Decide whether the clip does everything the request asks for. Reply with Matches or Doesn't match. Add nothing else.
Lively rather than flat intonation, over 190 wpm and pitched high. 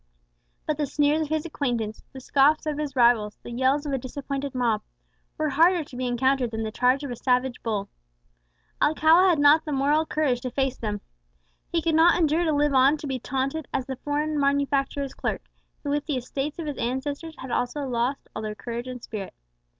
Doesn't match